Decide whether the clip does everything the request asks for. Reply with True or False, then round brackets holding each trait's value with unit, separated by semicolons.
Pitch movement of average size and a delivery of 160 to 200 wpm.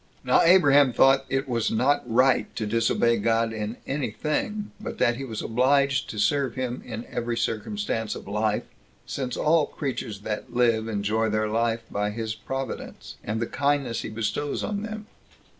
True (3.7 semitones; 175 wpm)